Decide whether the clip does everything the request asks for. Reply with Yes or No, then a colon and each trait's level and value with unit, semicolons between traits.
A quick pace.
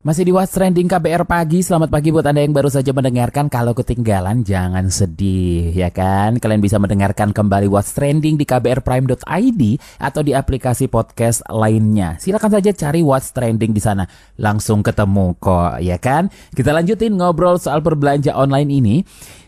Yes: fast, 160 wpm